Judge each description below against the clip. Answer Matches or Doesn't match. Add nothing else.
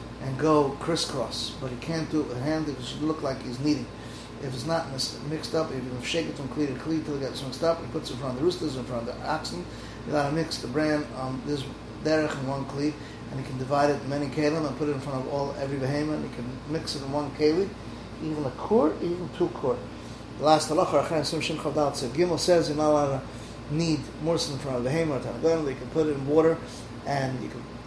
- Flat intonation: Doesn't match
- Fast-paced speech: Matches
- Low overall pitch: Doesn't match